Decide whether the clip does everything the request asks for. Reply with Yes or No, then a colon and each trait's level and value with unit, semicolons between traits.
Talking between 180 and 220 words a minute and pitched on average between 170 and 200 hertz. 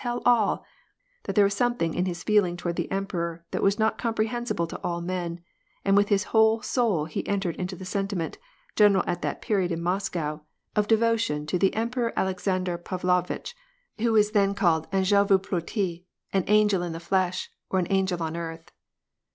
Yes: average, 185 wpm; high, 190 Hz